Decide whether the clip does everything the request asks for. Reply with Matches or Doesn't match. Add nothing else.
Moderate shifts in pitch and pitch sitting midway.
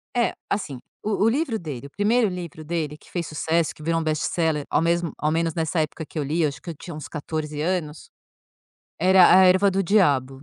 Matches